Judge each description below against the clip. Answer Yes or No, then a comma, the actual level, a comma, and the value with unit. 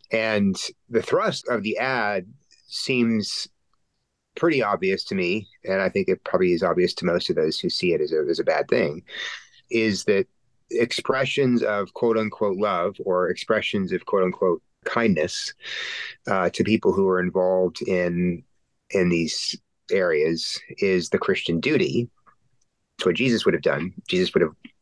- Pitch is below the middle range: Yes, low, 115 Hz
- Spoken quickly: No, average, 160 wpm